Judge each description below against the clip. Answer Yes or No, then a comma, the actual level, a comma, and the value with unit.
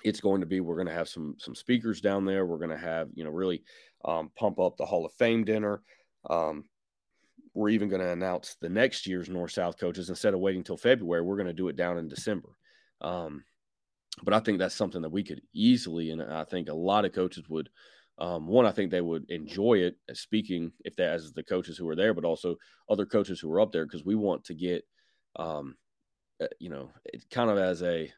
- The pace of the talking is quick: Yes, fast, 230 wpm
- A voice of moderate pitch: No, very low, 90 Hz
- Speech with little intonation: No, average, 3.6 semitones